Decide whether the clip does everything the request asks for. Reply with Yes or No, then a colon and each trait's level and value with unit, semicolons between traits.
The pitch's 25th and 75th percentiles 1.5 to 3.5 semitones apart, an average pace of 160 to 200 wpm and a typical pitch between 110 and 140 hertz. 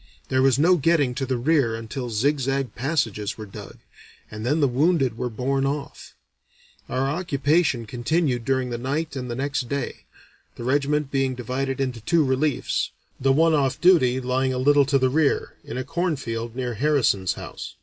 Yes: average, 2.7 semitones; average, 180 wpm; low, 135 Hz